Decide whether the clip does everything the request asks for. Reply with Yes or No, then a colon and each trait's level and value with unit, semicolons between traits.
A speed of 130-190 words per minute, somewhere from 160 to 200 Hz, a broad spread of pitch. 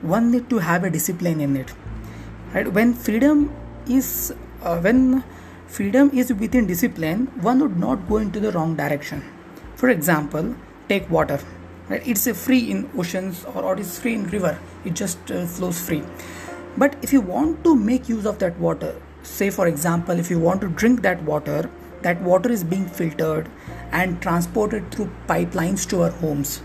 Yes: average, 180 wpm; high, 190 Hz; wide, 5.8 semitones